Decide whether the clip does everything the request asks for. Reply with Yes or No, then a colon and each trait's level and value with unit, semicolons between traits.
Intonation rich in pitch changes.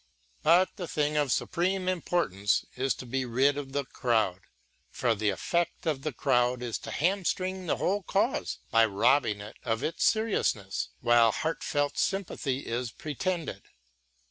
Yes: wide, 6.6 semitones